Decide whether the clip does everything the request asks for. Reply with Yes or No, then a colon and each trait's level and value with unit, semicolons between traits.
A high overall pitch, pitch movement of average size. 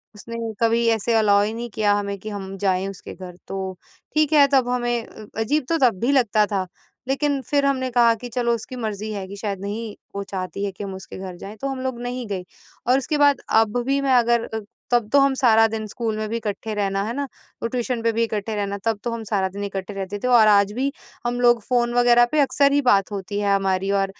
Yes: high, 225 Hz; average, 3.5 semitones